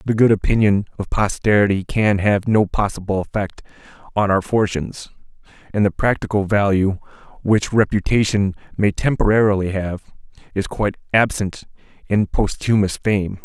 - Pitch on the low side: Yes, low, 100 Hz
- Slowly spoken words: Yes, slow, 125 wpm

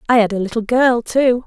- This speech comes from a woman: Yes, female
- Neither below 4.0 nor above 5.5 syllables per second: Yes, 5.4 syllables/s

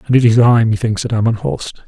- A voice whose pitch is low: Yes, low, 115 Hz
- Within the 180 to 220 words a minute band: No, fast, 255 wpm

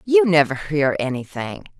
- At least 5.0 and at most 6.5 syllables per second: No, 4.5 syllables/s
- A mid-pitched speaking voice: Yes, medium, 160 Hz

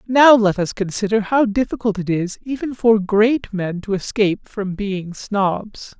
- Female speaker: No, male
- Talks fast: No, average, 170 wpm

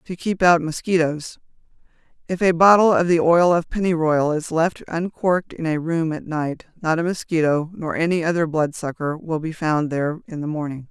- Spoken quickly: No, average, 185 wpm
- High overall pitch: No, medium, 165 Hz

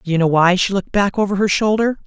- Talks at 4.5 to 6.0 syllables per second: No, 6.2 syllables/s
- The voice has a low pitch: No, high, 195 Hz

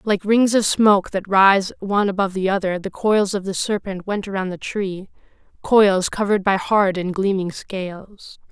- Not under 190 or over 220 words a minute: No, average, 175 wpm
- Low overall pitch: No, high, 195 Hz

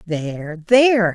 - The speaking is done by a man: No, female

